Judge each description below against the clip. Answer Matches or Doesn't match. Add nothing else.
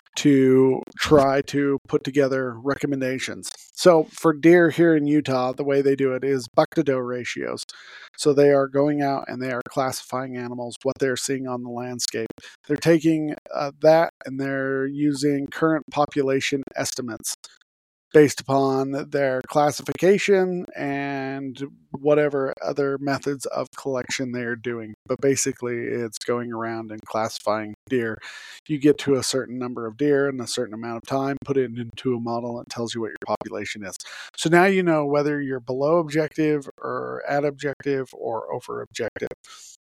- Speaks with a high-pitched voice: Doesn't match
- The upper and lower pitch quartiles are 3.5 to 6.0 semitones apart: Doesn't match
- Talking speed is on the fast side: Doesn't match